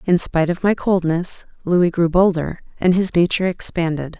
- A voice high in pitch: No, medium, 175 Hz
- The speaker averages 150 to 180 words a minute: Yes, average, 170 wpm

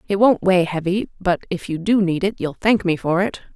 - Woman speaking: Yes, female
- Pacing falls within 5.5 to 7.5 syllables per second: No, 5.3 syllables/s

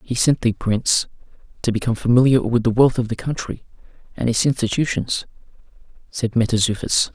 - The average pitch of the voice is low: Yes, low, 120 Hz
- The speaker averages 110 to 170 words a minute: Yes, average, 150 wpm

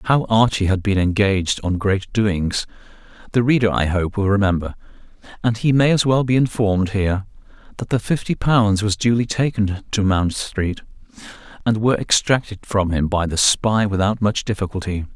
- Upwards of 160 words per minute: Yes, average, 170 wpm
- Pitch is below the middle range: Yes, low, 105 Hz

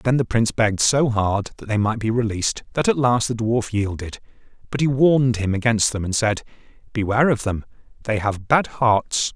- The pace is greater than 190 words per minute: Yes, fast, 205 wpm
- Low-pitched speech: Yes, low, 115 Hz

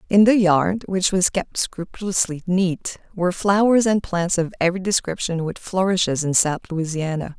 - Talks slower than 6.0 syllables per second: Yes, 4.9 syllables/s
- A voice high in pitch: No, medium, 180 Hz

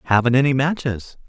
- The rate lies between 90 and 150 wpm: Yes, average, 140 wpm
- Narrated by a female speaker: No, male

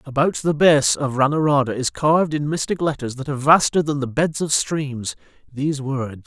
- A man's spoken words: Yes, male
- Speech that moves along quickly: No, average, 190 wpm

